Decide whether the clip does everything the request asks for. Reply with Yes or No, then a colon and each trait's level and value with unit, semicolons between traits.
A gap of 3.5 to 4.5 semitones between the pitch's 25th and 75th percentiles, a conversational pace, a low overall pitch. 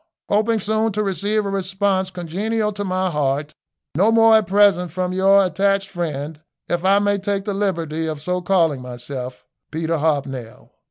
No: average, 4.1 semitones; average, 165 wpm; medium, 185 Hz